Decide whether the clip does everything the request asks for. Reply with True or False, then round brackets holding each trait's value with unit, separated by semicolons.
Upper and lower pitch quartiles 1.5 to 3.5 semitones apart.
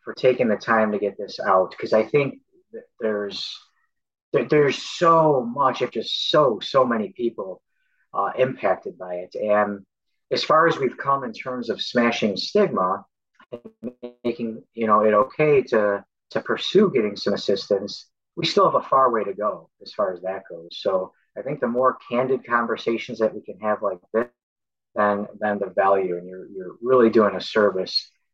False (3.9 semitones)